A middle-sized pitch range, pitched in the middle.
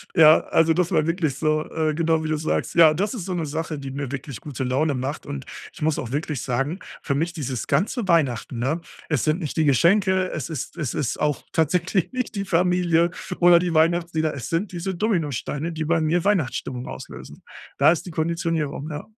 Yes: average, 3.1 semitones; medium, 160 Hz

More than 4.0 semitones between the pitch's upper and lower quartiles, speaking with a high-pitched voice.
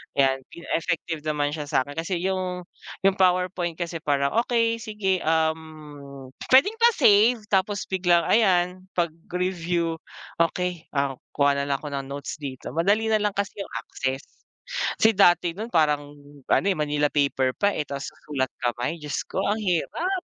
No: average, 5.0 semitones; medium, 170 Hz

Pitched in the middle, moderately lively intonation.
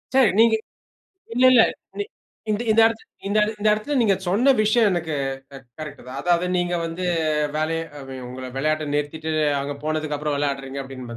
No: medium, 160 Hz; wide, 6.7 semitones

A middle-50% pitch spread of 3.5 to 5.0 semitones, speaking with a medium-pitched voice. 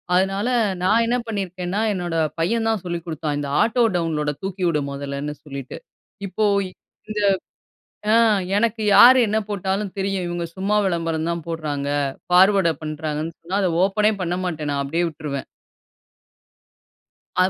Yes: average, 4.2 semitones; medium, 175 Hz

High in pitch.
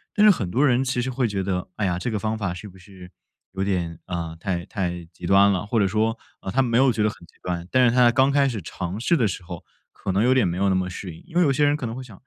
No: low, 100 Hz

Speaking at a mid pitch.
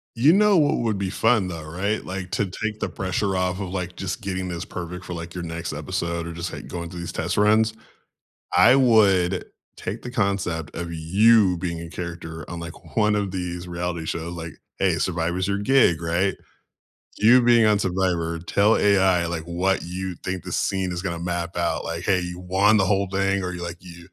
No: very low, 90 Hz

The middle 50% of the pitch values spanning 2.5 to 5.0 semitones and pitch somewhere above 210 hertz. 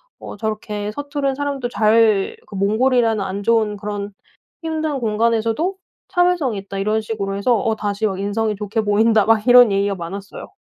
Yes: average, 3.1 semitones; high, 220 Hz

